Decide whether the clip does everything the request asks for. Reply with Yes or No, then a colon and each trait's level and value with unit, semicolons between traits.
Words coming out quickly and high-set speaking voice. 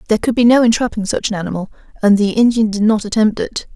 Yes: fast, 240 wpm; high, 215 Hz